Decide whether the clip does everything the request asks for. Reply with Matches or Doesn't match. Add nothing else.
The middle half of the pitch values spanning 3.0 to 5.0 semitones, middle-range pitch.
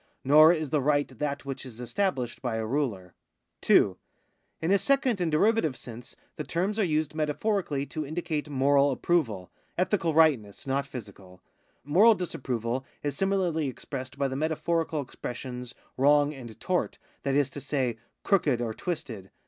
Matches